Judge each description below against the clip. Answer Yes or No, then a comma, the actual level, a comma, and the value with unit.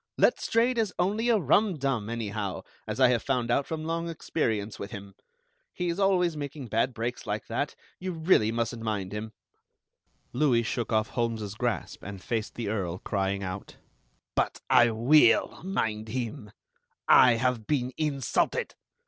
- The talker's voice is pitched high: No, low, 120 Hz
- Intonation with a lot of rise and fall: Yes, wide, 6.2 semitones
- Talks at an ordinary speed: Yes, average, 150 wpm